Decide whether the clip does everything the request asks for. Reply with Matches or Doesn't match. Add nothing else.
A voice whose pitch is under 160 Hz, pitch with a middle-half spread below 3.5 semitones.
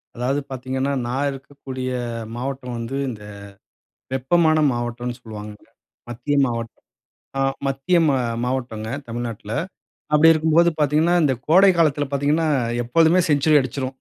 Doesn't match